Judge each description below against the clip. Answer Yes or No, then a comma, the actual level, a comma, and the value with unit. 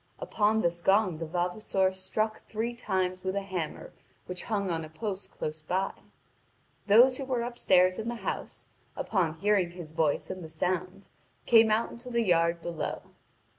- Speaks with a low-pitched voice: No, high, 190 Hz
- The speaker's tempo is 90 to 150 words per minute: No, average, 170 wpm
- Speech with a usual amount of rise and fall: Yes, average, 4.0 semitones